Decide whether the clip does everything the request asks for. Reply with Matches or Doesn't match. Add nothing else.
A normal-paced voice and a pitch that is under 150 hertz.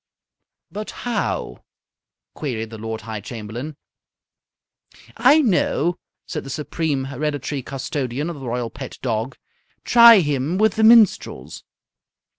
Doesn't match